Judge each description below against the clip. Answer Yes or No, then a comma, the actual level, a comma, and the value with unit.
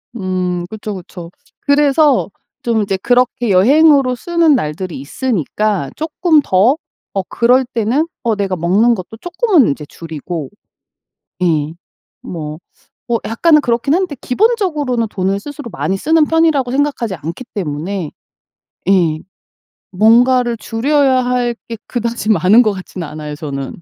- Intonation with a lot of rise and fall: Yes, wide, 6.9 semitones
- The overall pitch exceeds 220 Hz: Yes, high, 230 Hz